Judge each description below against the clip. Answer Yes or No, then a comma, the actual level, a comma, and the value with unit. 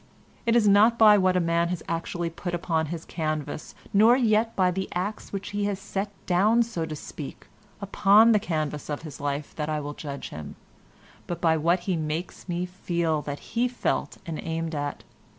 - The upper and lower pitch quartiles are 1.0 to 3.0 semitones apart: No, average, 4.4 semitones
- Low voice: No, medium, 175 Hz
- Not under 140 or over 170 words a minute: No, average, 195 wpm